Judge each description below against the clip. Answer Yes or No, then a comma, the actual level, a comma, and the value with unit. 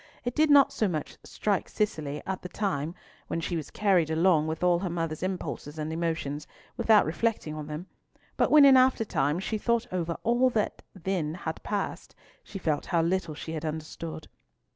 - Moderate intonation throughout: Yes, average, 4.7 semitones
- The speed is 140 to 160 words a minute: No, average, 185 wpm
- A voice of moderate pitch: Yes, medium, 170 Hz